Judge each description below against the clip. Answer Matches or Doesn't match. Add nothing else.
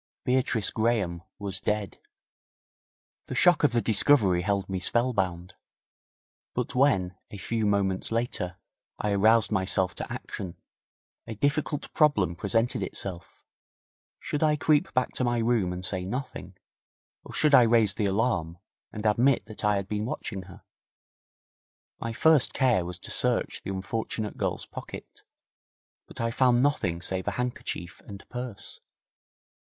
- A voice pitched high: Doesn't match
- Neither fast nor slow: Matches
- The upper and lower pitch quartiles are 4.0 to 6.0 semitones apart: Matches